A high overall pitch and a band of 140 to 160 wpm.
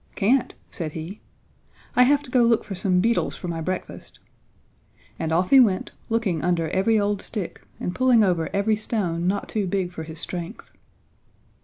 No: high, 195 Hz; average, 175 wpm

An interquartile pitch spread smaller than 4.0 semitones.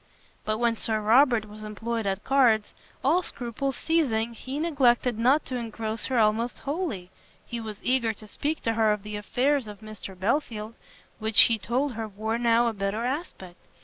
Yes: average, 3.2 semitones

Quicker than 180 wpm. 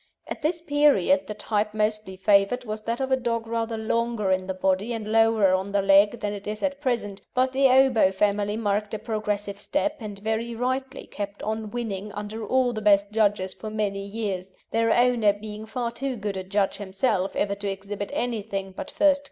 Yes: fast, 205 wpm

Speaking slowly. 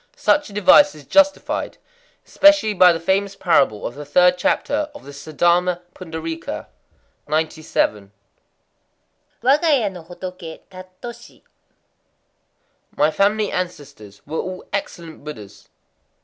Yes: slow, 110 wpm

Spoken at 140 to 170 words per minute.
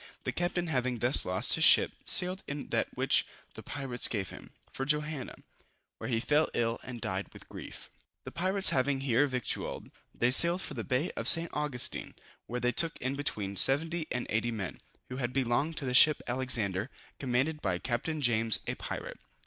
No: average, 185 wpm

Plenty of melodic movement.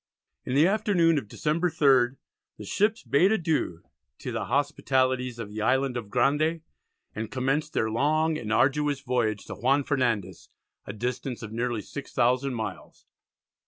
No: average, 4.0 semitones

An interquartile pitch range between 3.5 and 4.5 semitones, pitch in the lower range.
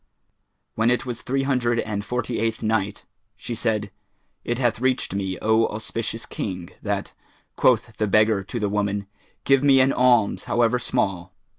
No: average, 3.1 semitones; low, 115 Hz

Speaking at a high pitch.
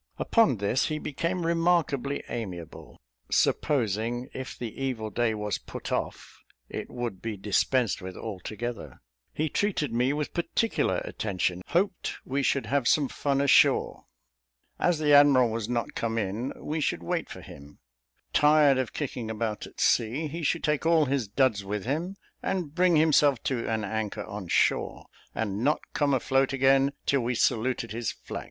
No: low, 130 Hz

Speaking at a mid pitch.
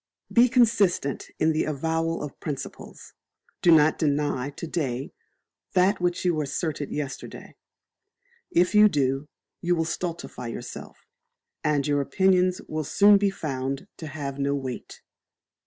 Yes: medium, 155 Hz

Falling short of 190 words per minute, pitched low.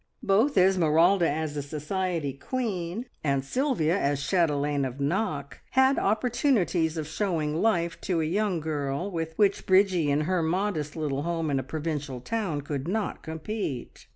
No: average, 155 wpm; medium, 165 Hz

